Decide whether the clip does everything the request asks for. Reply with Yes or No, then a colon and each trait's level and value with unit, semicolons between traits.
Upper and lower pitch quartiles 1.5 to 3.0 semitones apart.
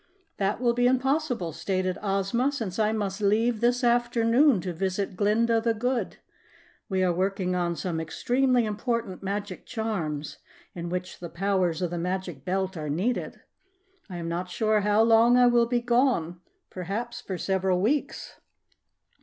No: average, 4.6 semitones